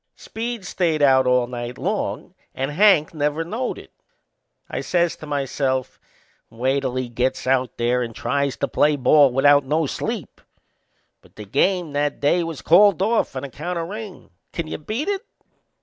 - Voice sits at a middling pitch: Yes, medium, 145 Hz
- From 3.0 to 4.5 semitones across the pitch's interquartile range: No, average, 5.1 semitones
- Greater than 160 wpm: Yes, average, 170 wpm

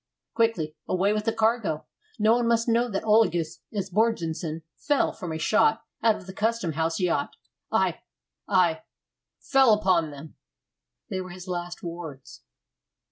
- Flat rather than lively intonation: No, average, 5.2 semitones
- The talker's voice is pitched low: No, high, 190 Hz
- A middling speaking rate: Yes, average, 145 wpm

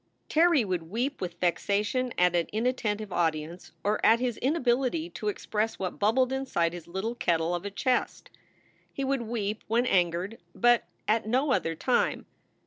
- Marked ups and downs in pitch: Yes, wide, 5.9 semitones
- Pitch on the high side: Yes, high, 215 Hz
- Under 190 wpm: Yes, average, 165 wpm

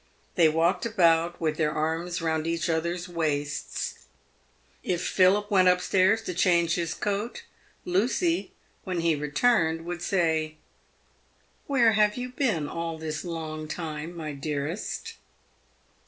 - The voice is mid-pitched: Yes, medium, 170 Hz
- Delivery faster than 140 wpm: No, slow, 135 wpm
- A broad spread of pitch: No, average, 3.0 semitones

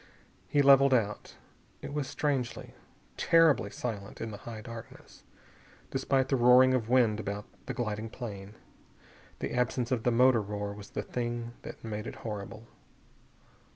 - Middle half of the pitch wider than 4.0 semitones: No, average, 3.4 semitones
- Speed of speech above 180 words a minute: No, average, 150 wpm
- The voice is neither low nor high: No, low, 115 Hz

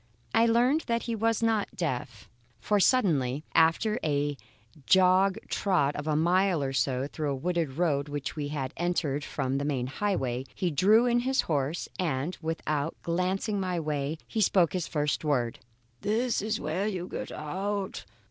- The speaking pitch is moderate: Yes, medium, 170 Hz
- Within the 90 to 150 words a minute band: No, average, 165 wpm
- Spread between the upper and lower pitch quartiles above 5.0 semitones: Yes, wide, 5.6 semitones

